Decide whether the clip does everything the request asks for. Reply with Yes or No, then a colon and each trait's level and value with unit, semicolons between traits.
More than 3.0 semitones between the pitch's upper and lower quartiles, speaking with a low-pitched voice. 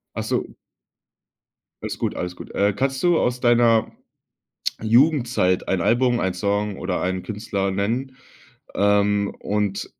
Yes: average, 3.6 semitones; low, 105 Hz